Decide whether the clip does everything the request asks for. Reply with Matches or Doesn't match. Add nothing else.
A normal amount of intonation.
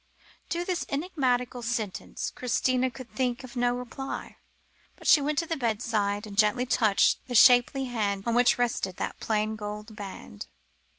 Matches